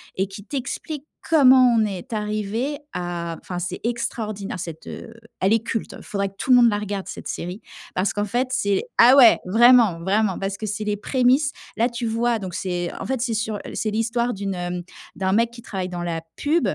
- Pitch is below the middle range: No, high, 215 Hz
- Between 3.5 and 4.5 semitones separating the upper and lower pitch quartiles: Yes, average, 4.0 semitones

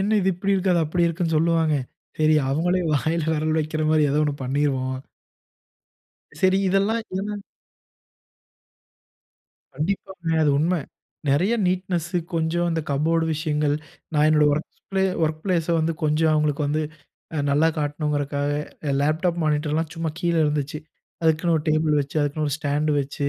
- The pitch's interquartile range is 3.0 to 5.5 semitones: No, narrow, 2.5 semitones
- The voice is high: No, medium, 155 Hz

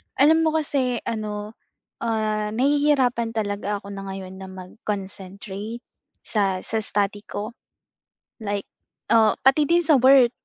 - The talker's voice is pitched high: Yes, high, 215 Hz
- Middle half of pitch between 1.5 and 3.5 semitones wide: No, average, 4.2 semitones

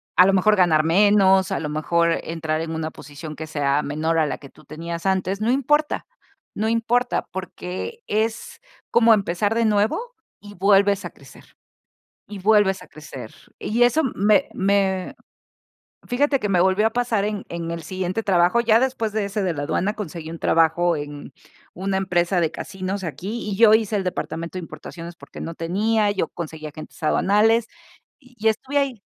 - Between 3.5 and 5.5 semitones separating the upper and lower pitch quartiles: Yes, average, 4.5 semitones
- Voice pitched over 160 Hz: Yes, high, 190 Hz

